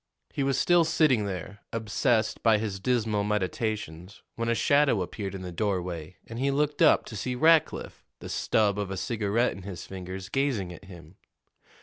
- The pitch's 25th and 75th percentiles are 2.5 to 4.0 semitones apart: No, average, 4.7 semitones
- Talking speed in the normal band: Yes, average, 180 wpm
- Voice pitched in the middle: No, low, 105 Hz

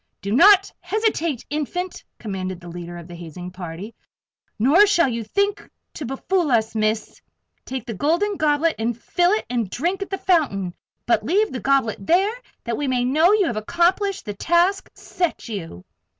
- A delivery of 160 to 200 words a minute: Yes, average, 170 wpm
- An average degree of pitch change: No, wide, 8.9 semitones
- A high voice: Yes, very high, 270 Hz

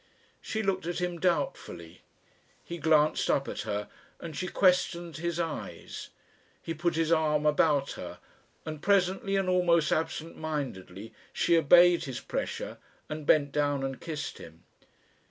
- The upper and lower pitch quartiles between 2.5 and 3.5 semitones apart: Yes, average, 3.1 semitones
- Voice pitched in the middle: Yes, medium, 160 Hz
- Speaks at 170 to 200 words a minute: No, average, 145 wpm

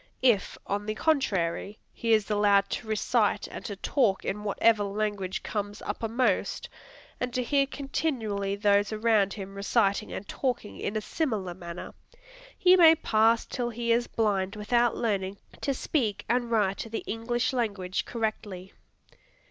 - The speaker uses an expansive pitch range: No, average, 3.1 semitones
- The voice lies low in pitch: No, high, 215 Hz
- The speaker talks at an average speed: Yes, average, 150 wpm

